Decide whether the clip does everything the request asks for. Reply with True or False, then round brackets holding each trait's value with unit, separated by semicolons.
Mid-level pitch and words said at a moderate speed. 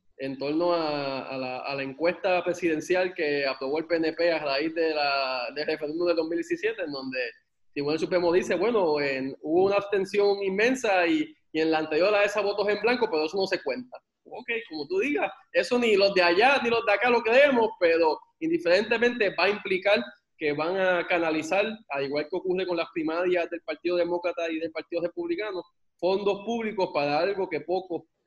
False (175 Hz; 195 wpm)